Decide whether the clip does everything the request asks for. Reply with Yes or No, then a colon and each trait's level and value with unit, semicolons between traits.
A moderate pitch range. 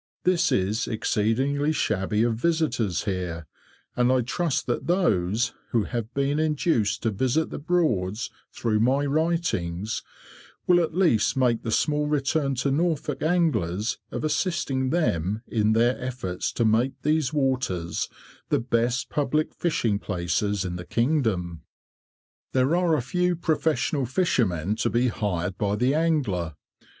No: wide, 6.6 semitones